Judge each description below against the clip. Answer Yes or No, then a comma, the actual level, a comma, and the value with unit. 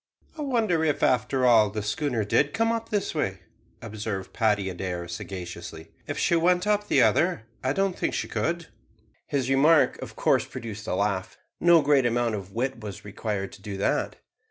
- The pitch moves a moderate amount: No, wide, 8.3 semitones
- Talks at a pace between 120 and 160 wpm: No, average, 180 wpm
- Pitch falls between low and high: No, low, 120 Hz